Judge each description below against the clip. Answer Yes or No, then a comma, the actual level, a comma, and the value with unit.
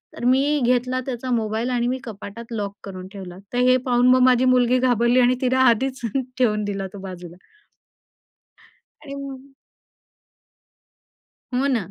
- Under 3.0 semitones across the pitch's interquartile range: No, average, 3.4 semitones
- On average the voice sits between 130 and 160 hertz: No, high, 245 Hz